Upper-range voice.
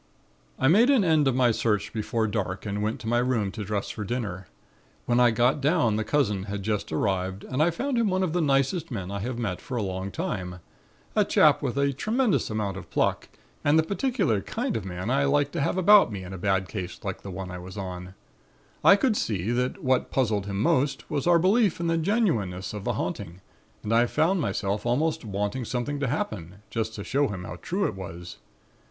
No: low, 120 Hz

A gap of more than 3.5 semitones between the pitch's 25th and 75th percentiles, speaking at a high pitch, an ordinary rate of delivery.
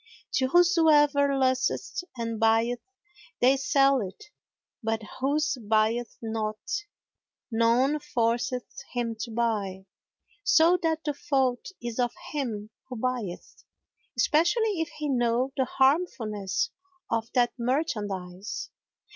No: average, 4.1 semitones; very high, 250 Hz; slow, 110 wpm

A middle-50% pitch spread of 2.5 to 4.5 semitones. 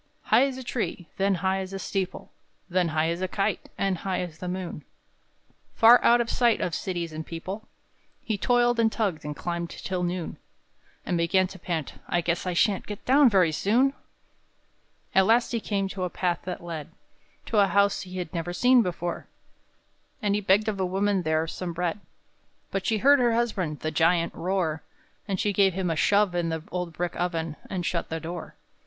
Yes: average, 3.2 semitones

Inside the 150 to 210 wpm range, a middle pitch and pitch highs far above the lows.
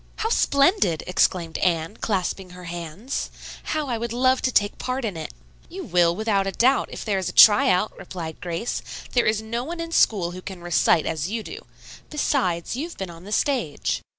No: average, 200 wpm; high, 200 Hz; wide, 6.3 semitones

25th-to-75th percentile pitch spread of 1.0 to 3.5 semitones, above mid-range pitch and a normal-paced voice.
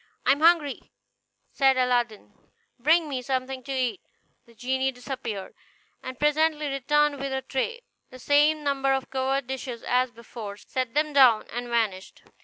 Yes: average, 2.7 semitones; very high, 265 Hz; average, 155 wpm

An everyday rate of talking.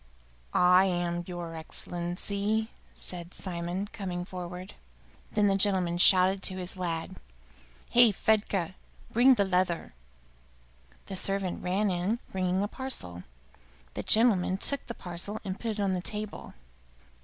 No: slow, 130 wpm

